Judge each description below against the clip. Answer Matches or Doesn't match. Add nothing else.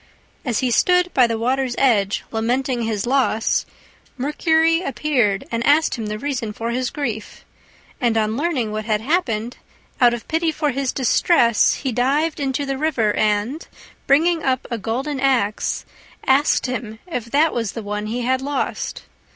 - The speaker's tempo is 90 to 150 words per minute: Doesn't match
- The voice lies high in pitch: Matches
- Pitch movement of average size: Matches